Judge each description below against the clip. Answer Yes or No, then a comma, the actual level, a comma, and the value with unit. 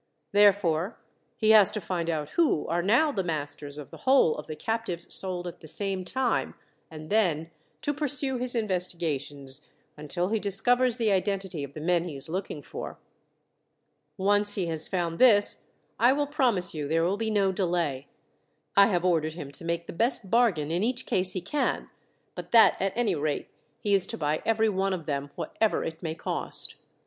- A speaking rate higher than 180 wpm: Yes, average, 190 wpm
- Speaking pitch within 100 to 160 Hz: No, medium, 185 Hz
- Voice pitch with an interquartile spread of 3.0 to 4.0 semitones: No, average, 5.2 semitones